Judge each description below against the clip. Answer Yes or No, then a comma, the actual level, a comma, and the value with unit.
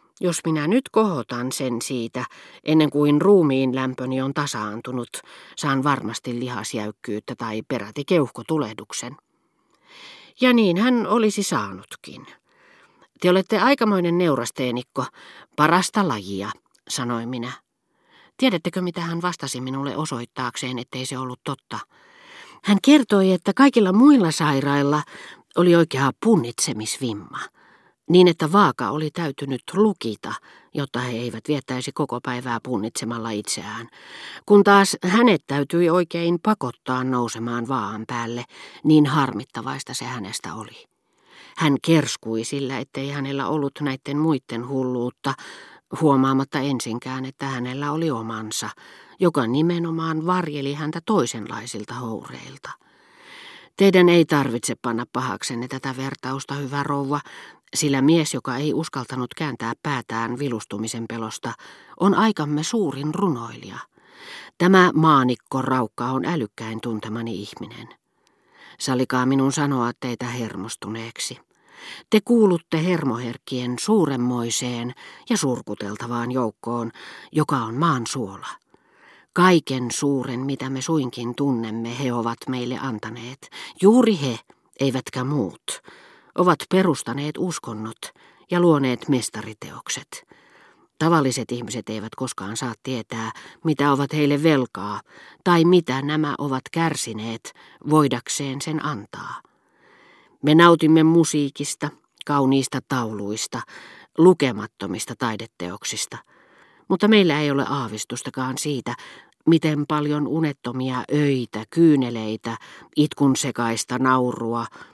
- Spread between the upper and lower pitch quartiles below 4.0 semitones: No, average, 5.0 semitones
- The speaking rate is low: No, average, 105 wpm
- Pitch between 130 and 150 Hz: Yes, low, 135 Hz